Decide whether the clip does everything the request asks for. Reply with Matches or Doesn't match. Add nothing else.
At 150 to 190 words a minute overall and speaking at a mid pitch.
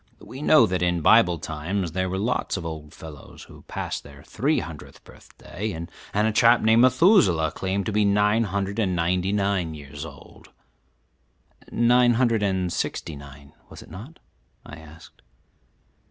Doesn't match